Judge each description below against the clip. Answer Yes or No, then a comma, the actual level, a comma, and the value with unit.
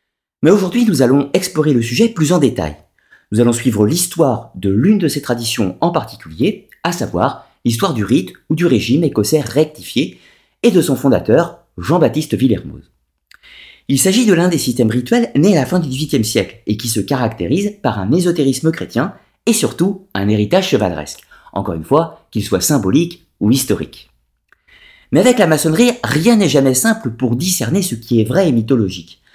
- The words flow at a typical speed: Yes, average, 180 wpm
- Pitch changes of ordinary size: No, wide, 8.1 semitones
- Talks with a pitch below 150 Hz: Yes, medium, 140 Hz